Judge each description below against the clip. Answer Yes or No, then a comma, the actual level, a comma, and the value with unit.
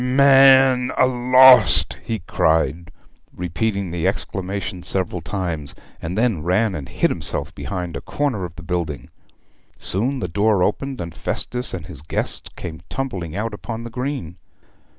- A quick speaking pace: No, average, 150 wpm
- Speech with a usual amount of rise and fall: No, wide, 6.7 semitones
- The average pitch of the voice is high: No, very low, 95 Hz